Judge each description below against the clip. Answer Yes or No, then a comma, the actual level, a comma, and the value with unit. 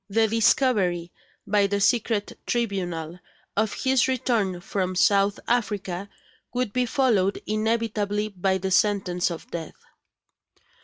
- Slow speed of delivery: Yes, slow, 115 wpm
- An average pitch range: Yes, average, 3.3 semitones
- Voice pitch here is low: No, high, 205 Hz